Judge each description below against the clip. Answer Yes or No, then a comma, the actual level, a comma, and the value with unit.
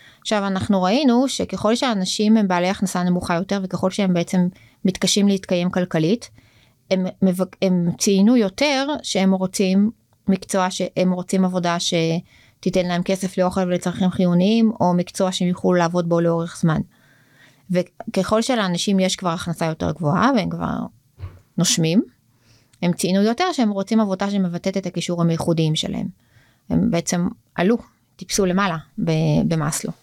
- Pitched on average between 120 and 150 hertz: No, medium, 185 Hz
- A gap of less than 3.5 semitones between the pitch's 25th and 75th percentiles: Yes, narrow, 2.6 semitones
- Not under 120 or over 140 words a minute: Yes, average, 135 wpm